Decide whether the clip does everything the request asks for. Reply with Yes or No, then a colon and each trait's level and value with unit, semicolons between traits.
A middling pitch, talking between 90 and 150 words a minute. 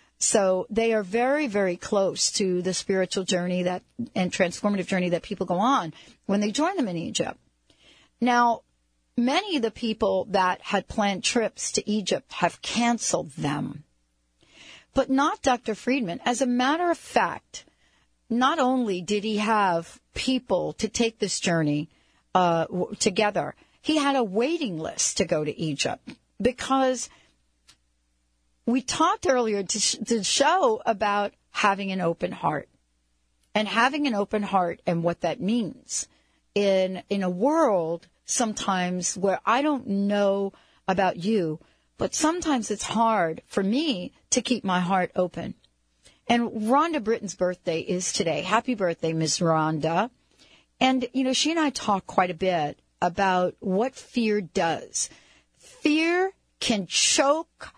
No: high, 205 Hz; average, 145 wpm